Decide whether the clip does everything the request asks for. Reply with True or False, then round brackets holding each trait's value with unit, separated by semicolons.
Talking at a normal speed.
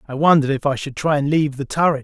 False (295 wpm)